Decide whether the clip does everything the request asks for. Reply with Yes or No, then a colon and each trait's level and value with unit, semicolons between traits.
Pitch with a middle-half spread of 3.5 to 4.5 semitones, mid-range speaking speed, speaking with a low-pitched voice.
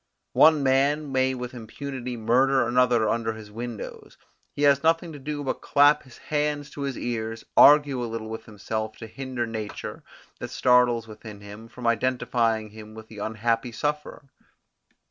Yes: average, 3.8 semitones; average, 165 wpm; low, 120 Hz